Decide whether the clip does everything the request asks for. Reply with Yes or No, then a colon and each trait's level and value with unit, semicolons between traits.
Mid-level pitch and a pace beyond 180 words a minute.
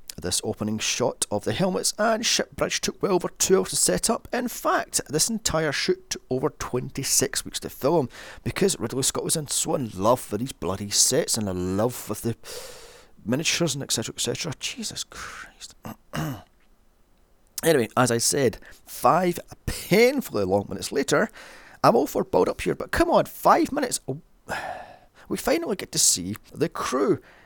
No: medium, 155 Hz; average, 175 wpm